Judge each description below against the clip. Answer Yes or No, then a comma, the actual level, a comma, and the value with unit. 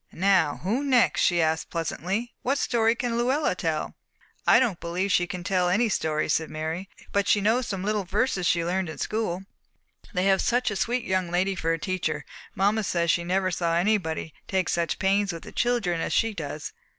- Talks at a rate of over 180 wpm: Yes, average, 200 wpm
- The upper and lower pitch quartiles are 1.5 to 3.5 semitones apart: No, average, 4.1 semitones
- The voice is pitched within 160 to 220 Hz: Yes, high, 190 Hz